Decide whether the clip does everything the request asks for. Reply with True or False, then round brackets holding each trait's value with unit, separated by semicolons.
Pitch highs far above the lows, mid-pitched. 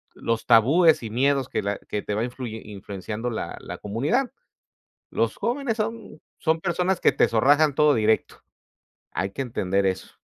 False (7.1 semitones; 125 Hz)